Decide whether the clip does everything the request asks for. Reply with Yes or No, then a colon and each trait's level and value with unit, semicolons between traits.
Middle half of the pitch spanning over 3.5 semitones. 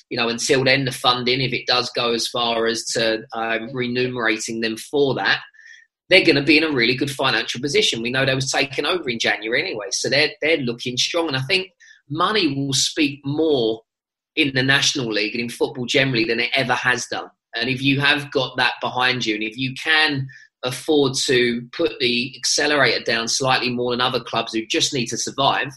No: average, 3.1 semitones